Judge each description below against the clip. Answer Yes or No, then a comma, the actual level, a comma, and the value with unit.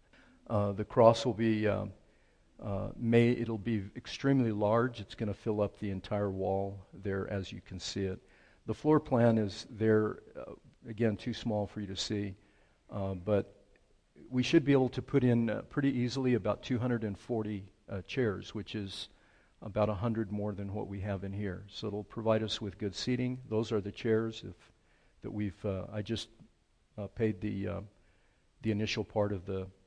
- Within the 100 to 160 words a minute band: No, average, 190 wpm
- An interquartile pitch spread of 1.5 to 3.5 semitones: Yes, narrow, 2.4 semitones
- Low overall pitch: Yes, low, 105 Hz